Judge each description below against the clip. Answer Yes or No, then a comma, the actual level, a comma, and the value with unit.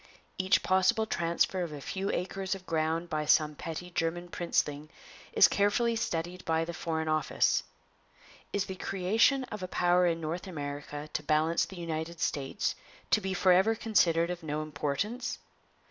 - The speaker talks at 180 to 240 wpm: No, average, 160 wpm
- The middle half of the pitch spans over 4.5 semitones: No, average, 3.2 semitones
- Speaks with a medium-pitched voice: Yes, medium, 170 Hz